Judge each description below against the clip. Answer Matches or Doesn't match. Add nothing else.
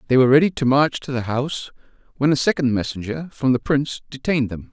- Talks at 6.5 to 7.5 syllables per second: Matches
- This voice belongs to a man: Matches